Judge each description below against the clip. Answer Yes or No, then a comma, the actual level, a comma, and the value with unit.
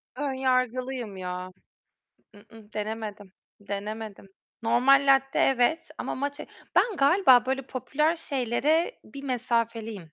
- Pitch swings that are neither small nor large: Yes, average, 4.1 semitones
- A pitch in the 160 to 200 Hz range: No, very high, 250 Hz